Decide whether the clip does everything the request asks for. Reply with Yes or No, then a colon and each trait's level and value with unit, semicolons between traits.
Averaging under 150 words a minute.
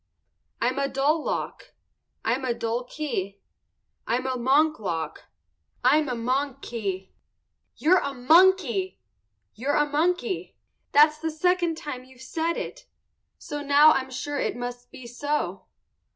Yes: average, 140 wpm